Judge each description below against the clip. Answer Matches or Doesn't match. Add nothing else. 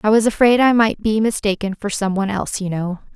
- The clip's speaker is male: Doesn't match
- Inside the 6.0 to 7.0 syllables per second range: Matches